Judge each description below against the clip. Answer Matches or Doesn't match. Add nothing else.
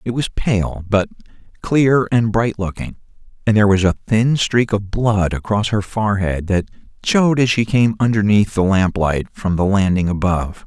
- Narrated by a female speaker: Doesn't match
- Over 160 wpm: Matches